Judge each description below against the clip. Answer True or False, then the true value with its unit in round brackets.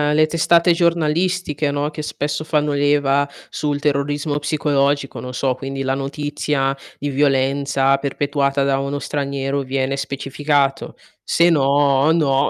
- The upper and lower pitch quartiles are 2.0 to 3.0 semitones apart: False (1.4 semitones)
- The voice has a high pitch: False (140 Hz)